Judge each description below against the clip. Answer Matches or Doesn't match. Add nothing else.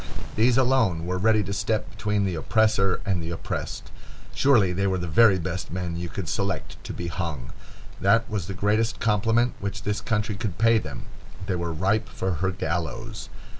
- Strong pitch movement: Doesn't match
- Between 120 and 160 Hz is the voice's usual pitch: Doesn't match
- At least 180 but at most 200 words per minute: Matches